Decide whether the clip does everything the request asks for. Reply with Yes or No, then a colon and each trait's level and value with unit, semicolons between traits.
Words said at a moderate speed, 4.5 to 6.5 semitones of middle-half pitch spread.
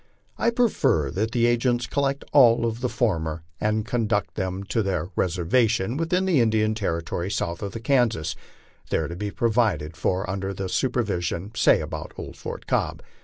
Yes: average, 165 wpm; average, 5.0 semitones